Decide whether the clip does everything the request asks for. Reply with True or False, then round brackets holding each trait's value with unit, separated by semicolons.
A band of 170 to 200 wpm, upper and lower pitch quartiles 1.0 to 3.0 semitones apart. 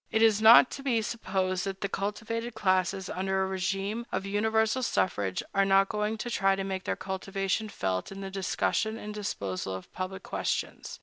True (185 wpm; 2.4 semitones)